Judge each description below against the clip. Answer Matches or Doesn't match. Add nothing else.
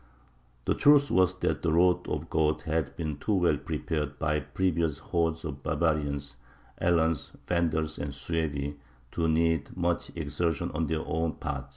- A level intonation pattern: Matches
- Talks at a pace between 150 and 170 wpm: Matches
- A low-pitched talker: Matches